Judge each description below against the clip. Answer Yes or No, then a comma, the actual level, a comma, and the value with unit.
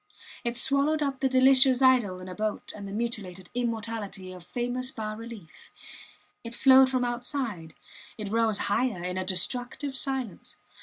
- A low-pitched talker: No, high, 235 Hz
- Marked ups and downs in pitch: No, average, 4.4 semitones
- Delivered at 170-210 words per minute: No, average, 155 wpm